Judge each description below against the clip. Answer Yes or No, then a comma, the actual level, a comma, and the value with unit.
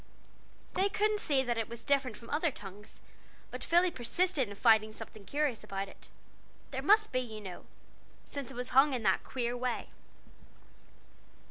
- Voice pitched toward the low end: No, very high, 250 Hz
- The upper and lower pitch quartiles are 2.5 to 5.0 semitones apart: No, wide, 5.4 semitones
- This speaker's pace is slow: No, average, 165 wpm